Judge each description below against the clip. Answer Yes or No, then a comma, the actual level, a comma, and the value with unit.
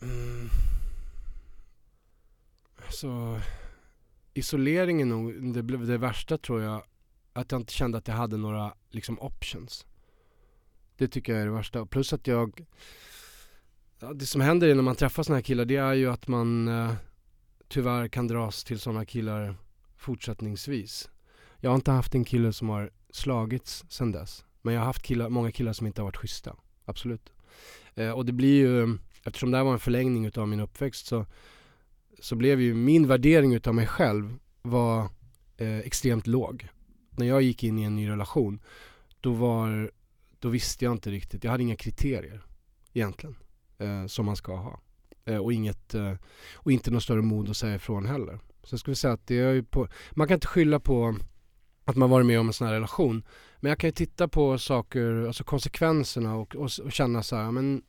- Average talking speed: Yes, average, 185 wpm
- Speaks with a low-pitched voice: Yes, low, 120 Hz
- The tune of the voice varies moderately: Yes, average, 3.2 semitones